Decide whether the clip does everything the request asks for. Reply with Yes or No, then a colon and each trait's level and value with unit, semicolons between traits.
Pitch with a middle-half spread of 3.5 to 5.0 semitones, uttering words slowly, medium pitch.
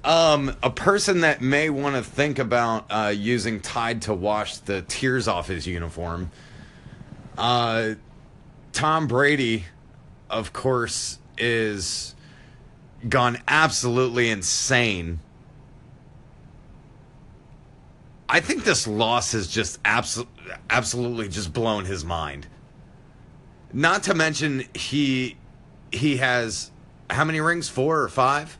No: average, 4.4 semitones; slow, 110 wpm; low, 120 Hz